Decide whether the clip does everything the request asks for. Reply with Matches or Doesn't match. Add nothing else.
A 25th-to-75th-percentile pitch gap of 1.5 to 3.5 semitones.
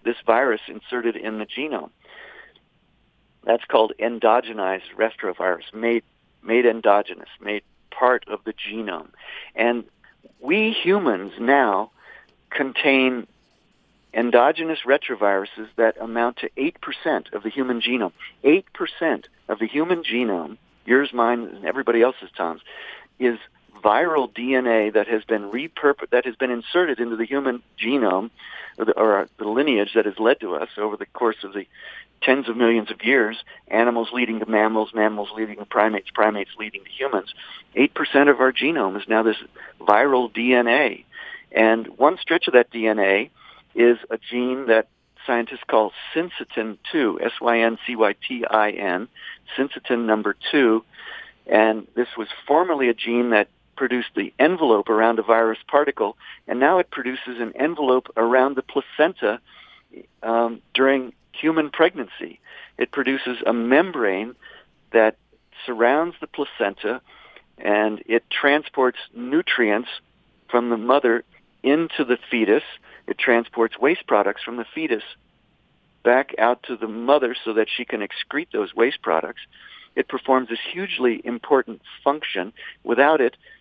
Matches